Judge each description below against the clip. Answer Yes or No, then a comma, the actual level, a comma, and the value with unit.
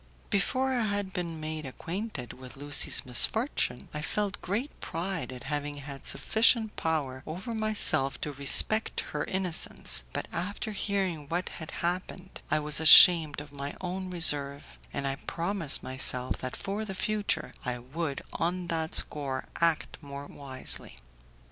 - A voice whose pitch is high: No, medium, 160 Hz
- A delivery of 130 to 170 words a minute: Yes, average, 150 wpm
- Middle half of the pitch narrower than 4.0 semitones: No, wide, 5.5 semitones